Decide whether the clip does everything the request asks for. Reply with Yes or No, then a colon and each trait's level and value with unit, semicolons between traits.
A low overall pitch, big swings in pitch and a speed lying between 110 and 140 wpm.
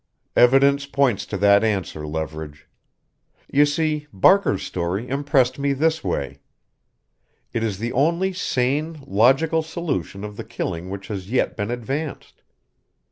Yes: low, 125 Hz; wide, 6.7 semitones; slow, 135 wpm